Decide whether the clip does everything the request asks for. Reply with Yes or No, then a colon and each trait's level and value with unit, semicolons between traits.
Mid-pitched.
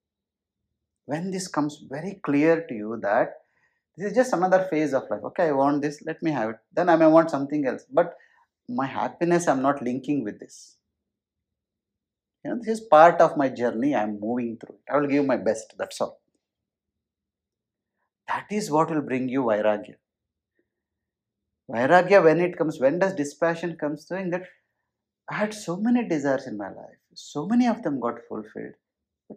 Yes: medium, 150 Hz